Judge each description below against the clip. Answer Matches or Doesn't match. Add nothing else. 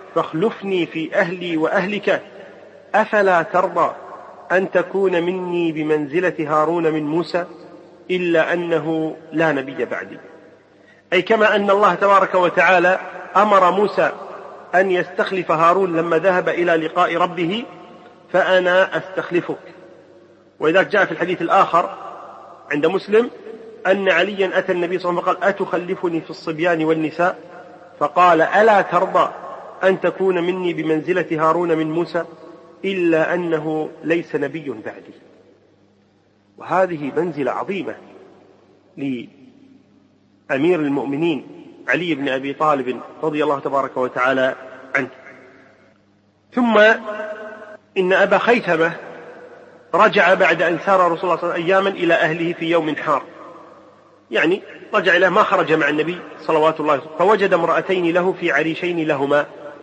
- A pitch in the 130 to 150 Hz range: Doesn't match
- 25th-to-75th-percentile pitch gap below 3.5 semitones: Matches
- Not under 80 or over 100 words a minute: Doesn't match